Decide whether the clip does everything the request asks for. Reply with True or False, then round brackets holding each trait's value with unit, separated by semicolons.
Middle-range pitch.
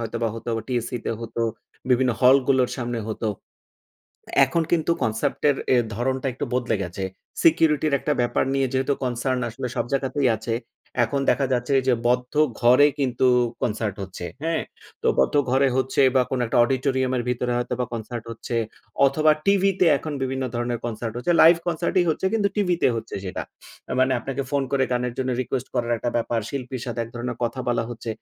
False (125 Hz)